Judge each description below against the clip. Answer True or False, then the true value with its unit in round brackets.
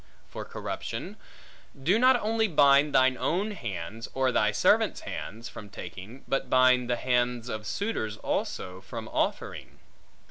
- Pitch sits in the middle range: False (125 Hz)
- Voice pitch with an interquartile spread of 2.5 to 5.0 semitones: False (5.4 semitones)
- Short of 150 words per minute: True (140 wpm)